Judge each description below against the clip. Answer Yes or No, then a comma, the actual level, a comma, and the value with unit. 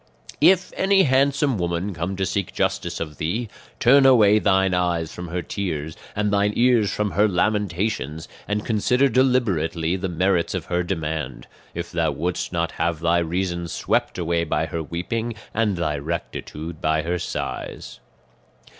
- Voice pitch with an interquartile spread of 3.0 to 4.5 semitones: Yes, average, 4.2 semitones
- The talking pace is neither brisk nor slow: Yes, average, 155 wpm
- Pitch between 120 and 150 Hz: No, very low, 90 Hz